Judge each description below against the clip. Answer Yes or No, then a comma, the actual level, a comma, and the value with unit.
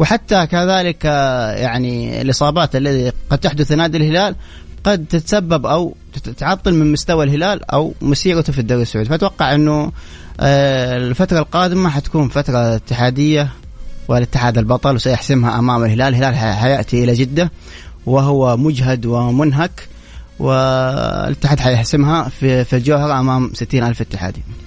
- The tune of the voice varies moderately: Yes, average, 4.1 semitones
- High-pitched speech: No, low, 135 Hz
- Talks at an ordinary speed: No, slow, 115 wpm